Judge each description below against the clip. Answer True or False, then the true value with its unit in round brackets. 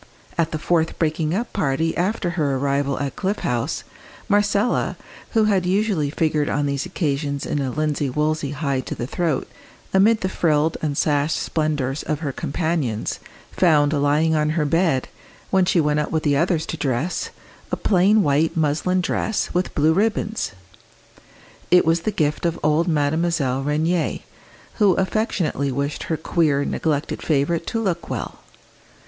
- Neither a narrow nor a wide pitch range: True (3.6 semitones)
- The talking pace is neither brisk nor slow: True (160 wpm)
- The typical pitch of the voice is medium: True (155 Hz)